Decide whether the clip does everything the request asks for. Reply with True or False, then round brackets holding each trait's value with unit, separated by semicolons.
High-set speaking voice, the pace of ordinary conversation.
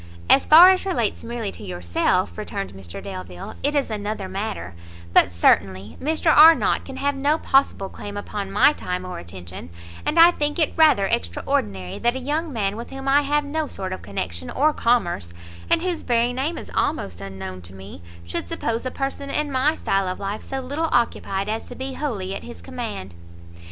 True (225 Hz; 190 wpm)